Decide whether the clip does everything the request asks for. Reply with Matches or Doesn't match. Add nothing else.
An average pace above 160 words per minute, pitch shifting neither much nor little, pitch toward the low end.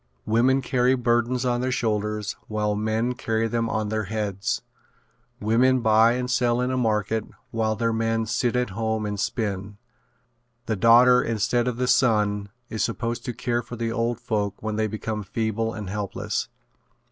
Doesn't match